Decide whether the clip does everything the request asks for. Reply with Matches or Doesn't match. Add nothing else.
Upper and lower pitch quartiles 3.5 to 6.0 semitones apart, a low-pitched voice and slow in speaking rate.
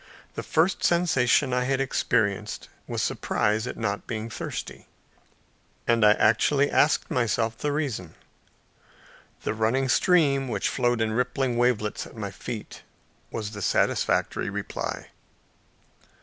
Matches